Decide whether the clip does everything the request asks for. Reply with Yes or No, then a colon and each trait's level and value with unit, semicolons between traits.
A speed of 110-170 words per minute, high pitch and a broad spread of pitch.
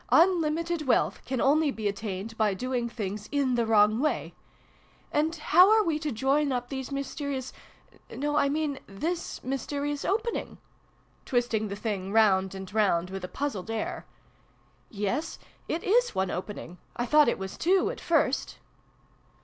Yes: average, 160 wpm; very high, 260 Hz; wide, 6.3 semitones